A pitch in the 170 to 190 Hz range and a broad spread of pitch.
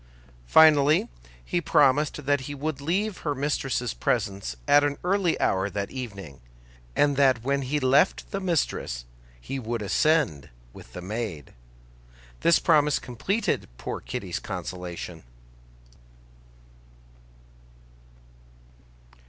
No: low, 135 Hz; wide, 7.0 semitones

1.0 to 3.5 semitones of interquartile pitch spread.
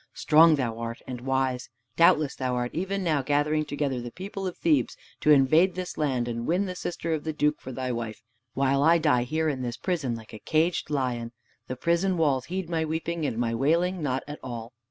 No: average, 4.8 semitones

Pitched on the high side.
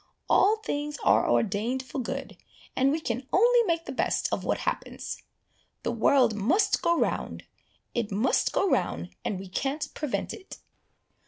Yes: very high, 270 Hz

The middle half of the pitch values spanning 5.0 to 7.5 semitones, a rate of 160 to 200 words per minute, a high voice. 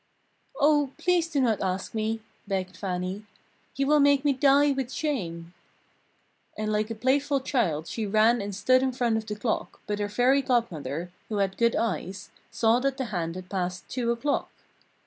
Yes: wide, 5.5 semitones; average, 180 wpm; high, 225 Hz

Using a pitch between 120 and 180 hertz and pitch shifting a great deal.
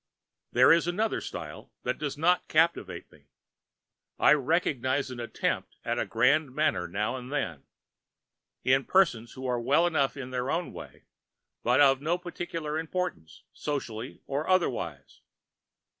No: medium, 140 Hz; average, 4.7 semitones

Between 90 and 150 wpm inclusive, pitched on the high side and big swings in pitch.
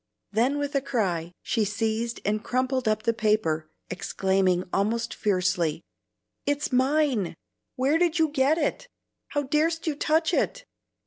Yes: average, 140 wpm; high, 235 Hz; wide, 6.4 semitones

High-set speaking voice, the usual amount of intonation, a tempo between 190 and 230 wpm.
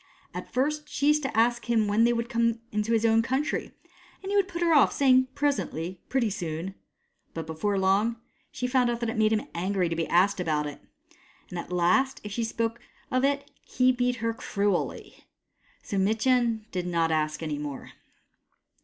No: high, 225 Hz; wide, 5.8 semitones; average, 195 wpm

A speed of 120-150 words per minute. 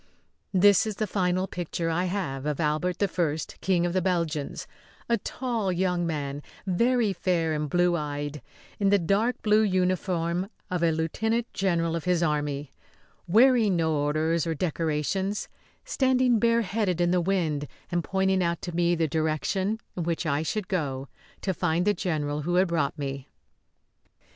No: average, 160 wpm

